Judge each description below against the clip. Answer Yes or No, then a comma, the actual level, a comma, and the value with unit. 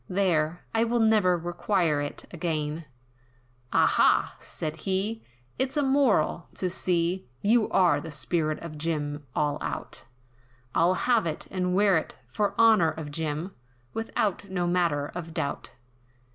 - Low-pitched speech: No, medium, 175 Hz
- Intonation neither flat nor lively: Yes, average, 4.5 semitones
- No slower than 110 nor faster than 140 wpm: Yes, slow, 135 wpm